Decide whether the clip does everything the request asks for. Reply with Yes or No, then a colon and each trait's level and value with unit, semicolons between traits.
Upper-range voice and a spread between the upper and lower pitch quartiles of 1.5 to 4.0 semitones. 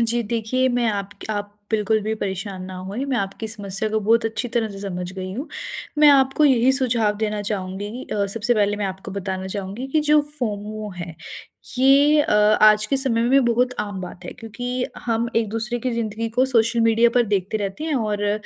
Yes: high, 220 Hz; average, 3.2 semitones